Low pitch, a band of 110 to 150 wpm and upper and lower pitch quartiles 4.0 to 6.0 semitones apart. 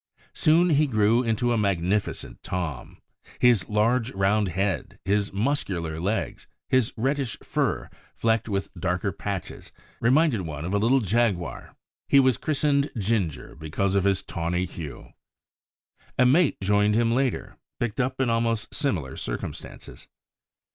Yes: low, 105 Hz; slow, 135 wpm; average, 4.8 semitones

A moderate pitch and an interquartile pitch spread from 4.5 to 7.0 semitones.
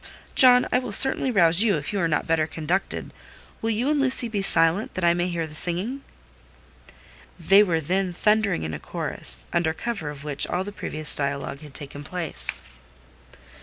Yes: medium, 175 Hz; wide, 5.4 semitones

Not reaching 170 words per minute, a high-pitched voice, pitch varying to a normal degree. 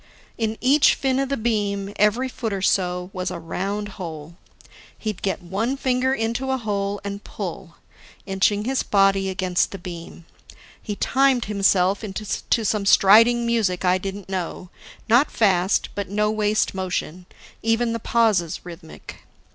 Yes: average, 150 wpm; high, 200 Hz; average, 3.4 semitones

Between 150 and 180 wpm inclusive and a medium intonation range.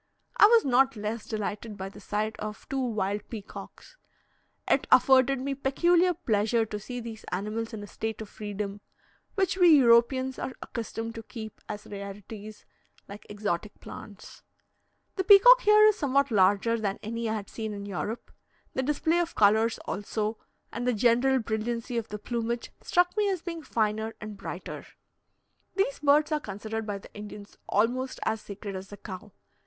Yes: average, 170 wpm; average, 4.2 semitones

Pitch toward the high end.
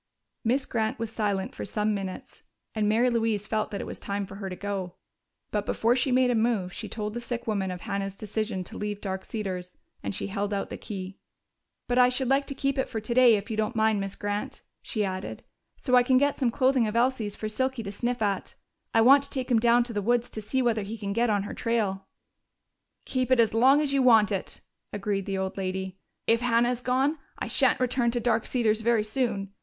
Yes: high, 220 Hz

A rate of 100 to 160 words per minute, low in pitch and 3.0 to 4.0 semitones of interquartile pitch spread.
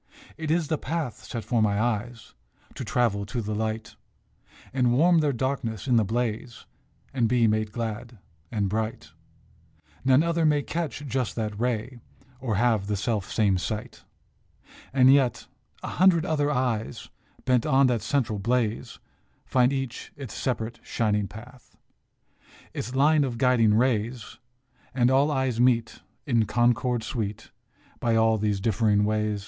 Yes: average, 150 wpm; low, 120 Hz; average, 3.3 semitones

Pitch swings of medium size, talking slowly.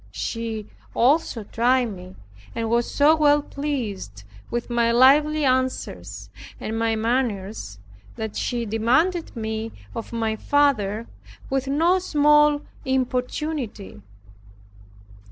Yes: average, 4.7 semitones; slow, 105 wpm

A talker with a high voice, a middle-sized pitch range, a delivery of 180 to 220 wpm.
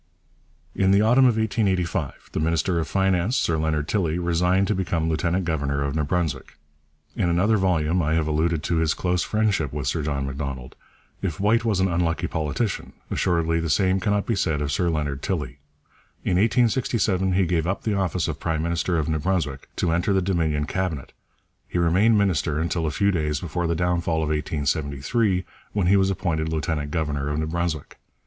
No: very low, 85 Hz; average, 3.6 semitones; average, 190 wpm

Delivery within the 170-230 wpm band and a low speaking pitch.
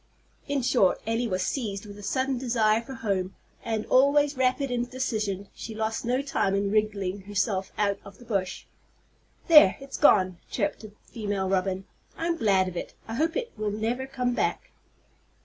No: average, 180 wpm; high, 220 Hz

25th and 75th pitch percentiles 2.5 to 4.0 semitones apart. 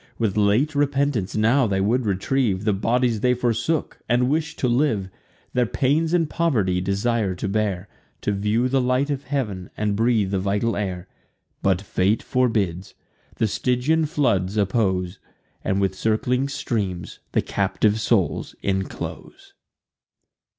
No: average, 4.5 semitones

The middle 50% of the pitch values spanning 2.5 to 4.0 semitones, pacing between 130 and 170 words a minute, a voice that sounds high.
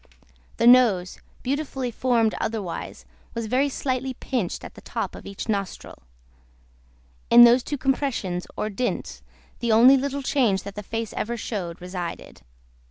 No: average, 4.4 semitones; average, 145 wpm; high, 235 Hz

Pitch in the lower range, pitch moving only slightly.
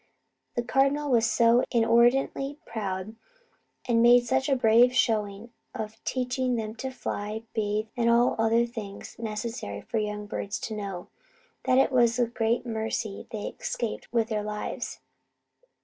No: high, 230 Hz; narrow, 2.3 semitones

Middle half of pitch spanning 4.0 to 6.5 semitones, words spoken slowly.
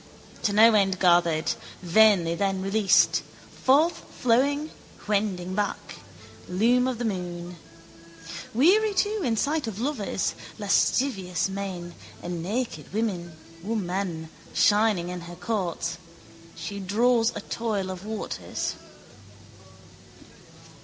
Yes: average, 4.5 semitones; slow, 100 wpm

